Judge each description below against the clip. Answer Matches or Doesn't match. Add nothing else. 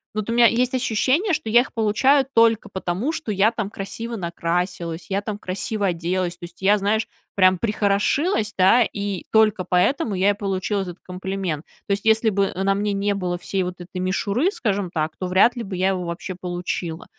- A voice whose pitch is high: Matches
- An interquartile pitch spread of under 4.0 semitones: Matches